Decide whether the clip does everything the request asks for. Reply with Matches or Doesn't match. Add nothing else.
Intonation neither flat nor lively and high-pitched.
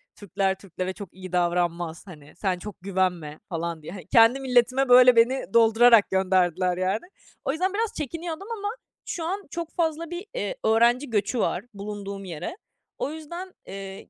Doesn't match